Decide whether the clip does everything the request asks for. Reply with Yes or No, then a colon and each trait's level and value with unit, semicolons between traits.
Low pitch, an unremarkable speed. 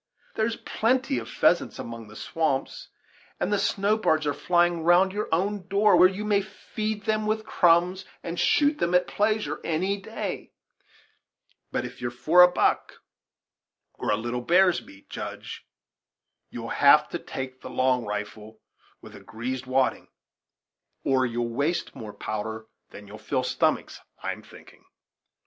No: medium, 170 Hz; average, 155 wpm